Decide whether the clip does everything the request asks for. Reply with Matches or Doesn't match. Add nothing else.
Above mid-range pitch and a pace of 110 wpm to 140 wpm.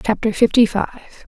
Matches